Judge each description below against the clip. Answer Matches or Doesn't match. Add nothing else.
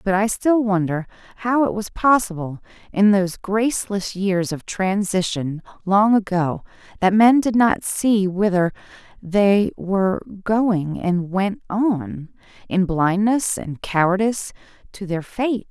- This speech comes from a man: Doesn't match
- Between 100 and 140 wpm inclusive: Matches